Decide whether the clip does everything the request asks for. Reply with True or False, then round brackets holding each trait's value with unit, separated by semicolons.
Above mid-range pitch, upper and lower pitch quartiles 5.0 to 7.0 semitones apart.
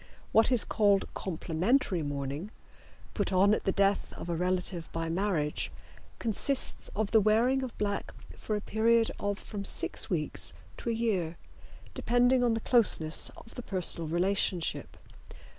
False (200 Hz; 4.6 semitones)